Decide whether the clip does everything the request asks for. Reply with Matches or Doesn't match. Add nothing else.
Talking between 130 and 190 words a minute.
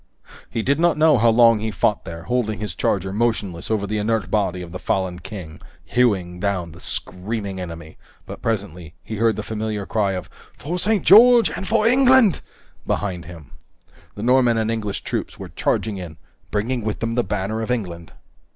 Matches